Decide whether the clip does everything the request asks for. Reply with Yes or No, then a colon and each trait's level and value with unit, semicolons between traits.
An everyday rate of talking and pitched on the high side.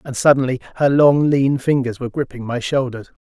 No: average, 185 wpm; low, 130 Hz